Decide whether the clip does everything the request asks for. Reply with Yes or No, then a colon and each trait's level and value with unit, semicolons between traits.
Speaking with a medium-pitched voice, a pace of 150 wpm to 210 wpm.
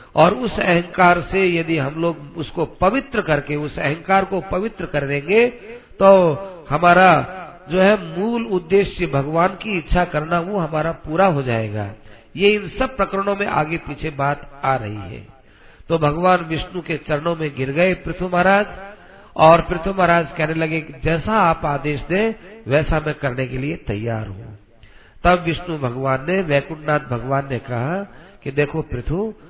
Yes: medium, 165 Hz; average, 160 wpm